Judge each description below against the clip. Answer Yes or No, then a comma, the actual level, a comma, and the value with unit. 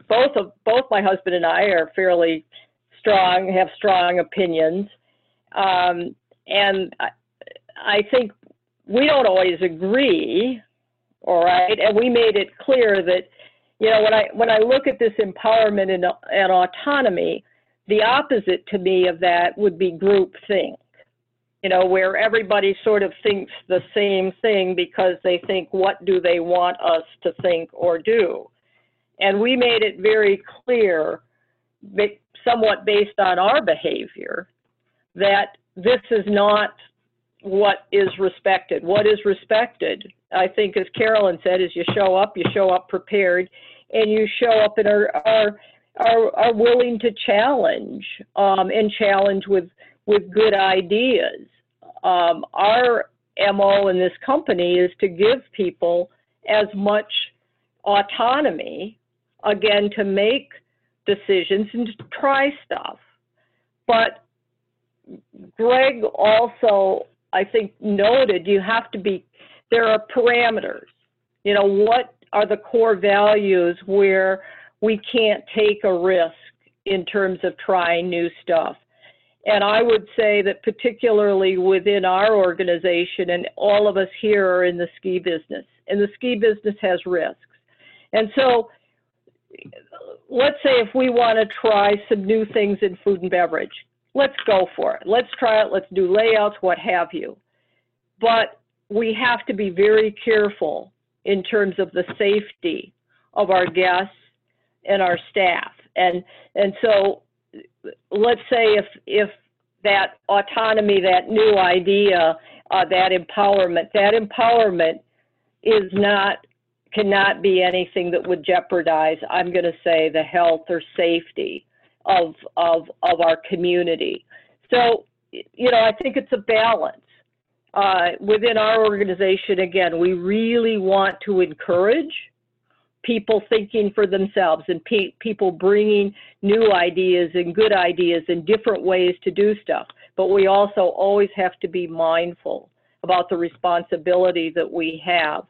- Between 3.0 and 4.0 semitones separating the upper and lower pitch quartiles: Yes, average, 3.4 semitones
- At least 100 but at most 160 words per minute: Yes, average, 140 wpm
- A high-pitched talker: Yes, high, 200 Hz